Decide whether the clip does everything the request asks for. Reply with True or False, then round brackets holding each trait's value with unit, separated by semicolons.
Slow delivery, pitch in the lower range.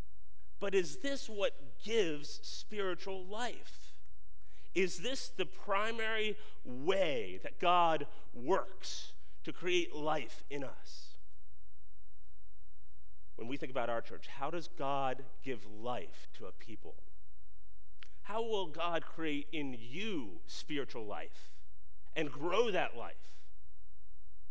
True (115 wpm; 120 Hz)